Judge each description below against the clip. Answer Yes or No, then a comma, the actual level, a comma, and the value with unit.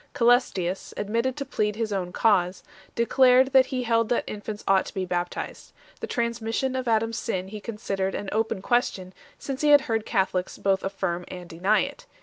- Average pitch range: Yes, average, 4.1 semitones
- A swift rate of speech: No, average, 190 wpm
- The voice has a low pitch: No, high, 215 Hz